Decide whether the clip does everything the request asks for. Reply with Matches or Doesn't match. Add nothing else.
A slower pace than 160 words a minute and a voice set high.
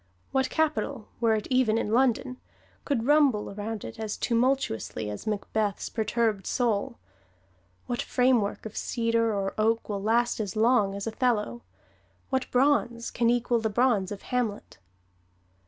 Matches